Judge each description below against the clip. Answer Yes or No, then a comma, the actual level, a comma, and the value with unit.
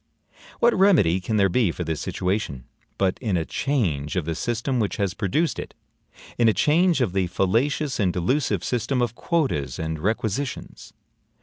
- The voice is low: Yes, low, 105 Hz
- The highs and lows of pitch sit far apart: Yes, wide, 7.0 semitones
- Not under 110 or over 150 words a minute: No, average, 170 wpm